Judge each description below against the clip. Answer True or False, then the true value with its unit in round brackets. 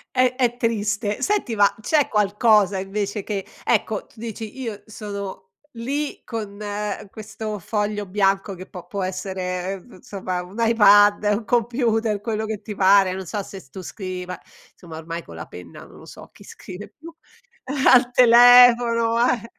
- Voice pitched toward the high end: True (210 Hz)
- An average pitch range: True (3.2 semitones)